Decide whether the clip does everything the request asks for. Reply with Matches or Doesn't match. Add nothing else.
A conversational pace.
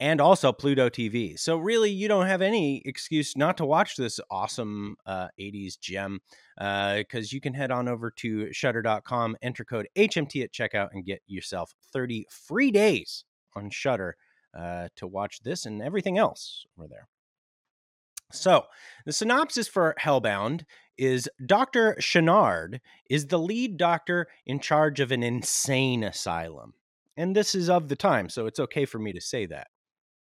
Matches